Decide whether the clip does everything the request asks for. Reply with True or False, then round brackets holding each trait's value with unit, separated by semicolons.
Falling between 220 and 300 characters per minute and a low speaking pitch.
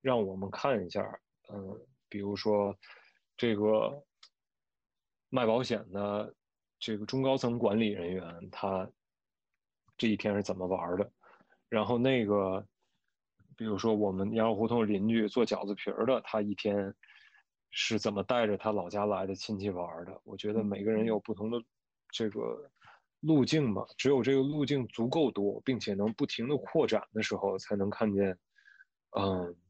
True (225 characters per minute; 105 Hz)